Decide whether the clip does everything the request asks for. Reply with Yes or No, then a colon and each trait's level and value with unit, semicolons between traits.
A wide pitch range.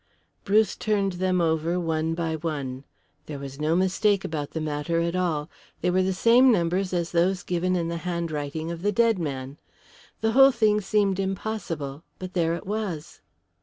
No: average, 3.5 semitones